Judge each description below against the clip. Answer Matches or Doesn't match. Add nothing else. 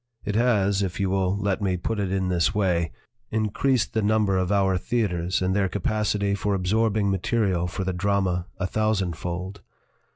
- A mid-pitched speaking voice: Doesn't match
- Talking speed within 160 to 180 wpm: Matches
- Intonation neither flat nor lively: Doesn't match